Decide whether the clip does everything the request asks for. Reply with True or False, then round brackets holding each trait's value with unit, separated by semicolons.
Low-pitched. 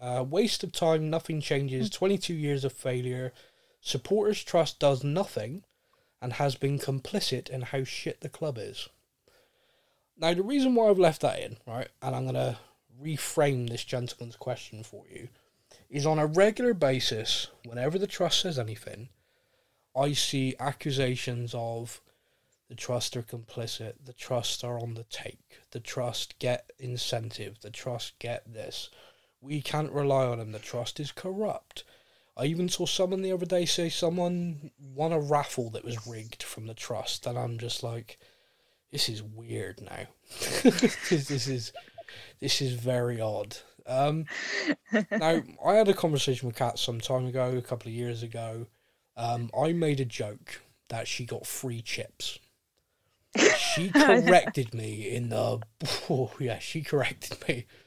True (130 Hz)